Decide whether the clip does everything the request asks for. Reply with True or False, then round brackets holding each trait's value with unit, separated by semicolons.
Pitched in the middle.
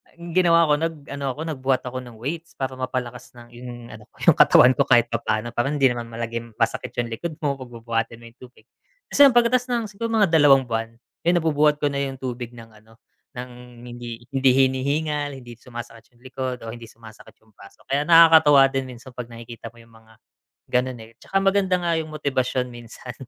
False (125 Hz)